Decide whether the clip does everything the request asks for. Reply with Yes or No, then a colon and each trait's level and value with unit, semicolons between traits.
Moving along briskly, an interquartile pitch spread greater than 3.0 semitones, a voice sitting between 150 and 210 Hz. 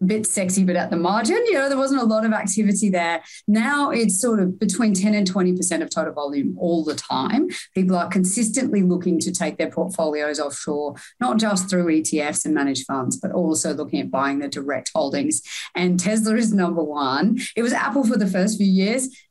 Yes: fast, 210 wpm; average, 5.1 semitones; high, 190 Hz